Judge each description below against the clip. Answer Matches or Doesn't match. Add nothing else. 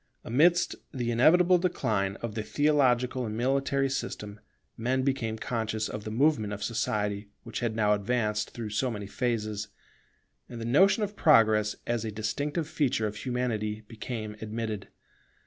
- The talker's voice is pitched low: Matches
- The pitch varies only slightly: Doesn't match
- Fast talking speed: Doesn't match